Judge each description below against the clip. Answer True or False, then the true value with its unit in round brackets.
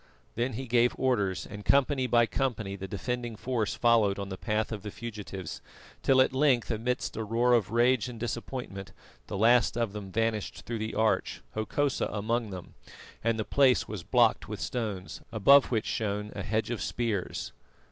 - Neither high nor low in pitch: False (115 Hz)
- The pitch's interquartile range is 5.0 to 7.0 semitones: False (2.9 semitones)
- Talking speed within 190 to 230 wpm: False (180 wpm)